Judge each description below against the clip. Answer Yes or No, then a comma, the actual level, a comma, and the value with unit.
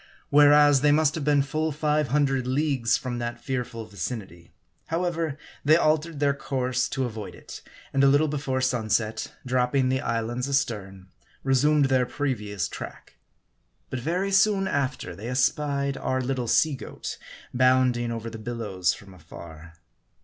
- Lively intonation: No, average, 3.9 semitones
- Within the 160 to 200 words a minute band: No, average, 150 wpm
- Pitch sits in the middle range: No, low, 130 Hz